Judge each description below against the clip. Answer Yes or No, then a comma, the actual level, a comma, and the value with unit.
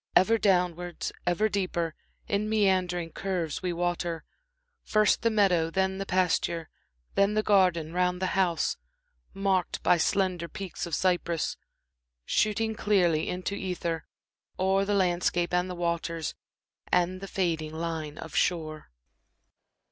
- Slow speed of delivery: Yes, slow, 130 wpm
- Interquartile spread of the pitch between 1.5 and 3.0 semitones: Yes, narrow, 2.4 semitones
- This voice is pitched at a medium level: Yes, medium, 180 Hz